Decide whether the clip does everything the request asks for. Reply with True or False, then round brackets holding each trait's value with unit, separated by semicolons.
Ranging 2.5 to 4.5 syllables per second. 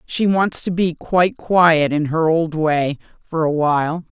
True (4.1 syllables/s)